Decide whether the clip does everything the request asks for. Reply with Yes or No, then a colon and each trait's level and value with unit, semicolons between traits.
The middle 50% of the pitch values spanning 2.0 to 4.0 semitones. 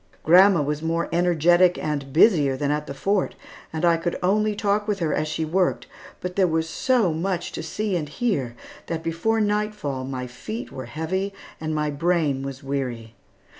No: average, 4.6 semitones